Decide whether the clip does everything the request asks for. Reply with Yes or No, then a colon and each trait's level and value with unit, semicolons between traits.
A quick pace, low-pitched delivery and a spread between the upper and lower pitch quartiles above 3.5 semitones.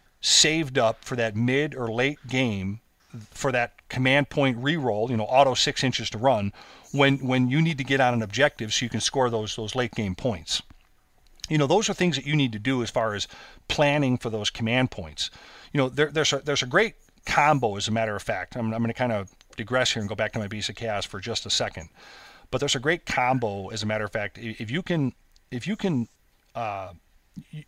Yes: fast, 230 wpm; low, 125 Hz; average, 4.1 semitones